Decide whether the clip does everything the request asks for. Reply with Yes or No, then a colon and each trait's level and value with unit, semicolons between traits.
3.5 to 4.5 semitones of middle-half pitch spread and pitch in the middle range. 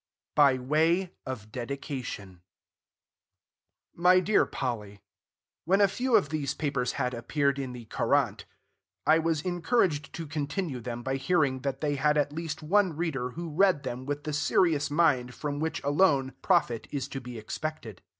Yes: average, 4.1 semitones; medium, 145 Hz